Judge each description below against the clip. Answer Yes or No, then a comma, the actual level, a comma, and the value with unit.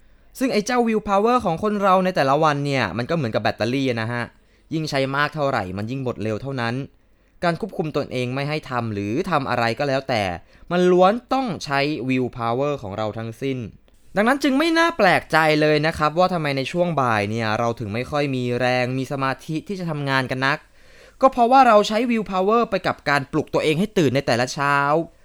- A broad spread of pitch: Yes, wide, 6.8 semitones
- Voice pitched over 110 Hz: Yes, medium, 140 Hz